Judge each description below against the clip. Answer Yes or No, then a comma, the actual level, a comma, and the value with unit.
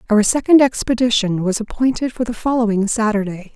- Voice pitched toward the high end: Yes, high, 225 Hz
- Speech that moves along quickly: No, average, 150 wpm